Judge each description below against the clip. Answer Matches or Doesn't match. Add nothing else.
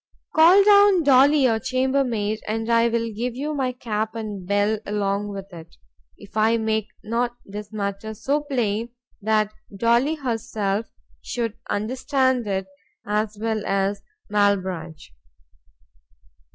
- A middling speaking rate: Doesn't match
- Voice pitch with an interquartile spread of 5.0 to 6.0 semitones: Doesn't match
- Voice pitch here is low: Doesn't match